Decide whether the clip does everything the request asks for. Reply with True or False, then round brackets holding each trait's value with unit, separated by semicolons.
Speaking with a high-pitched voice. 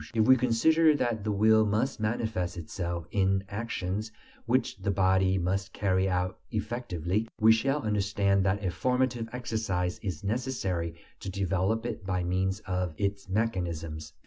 False (100 Hz)